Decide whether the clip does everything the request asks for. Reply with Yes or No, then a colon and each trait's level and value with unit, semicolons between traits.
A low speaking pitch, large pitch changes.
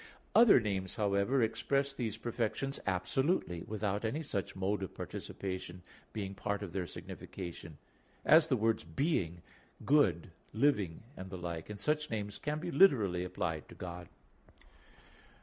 Yes: low, 100 Hz; wide, 6.4 semitones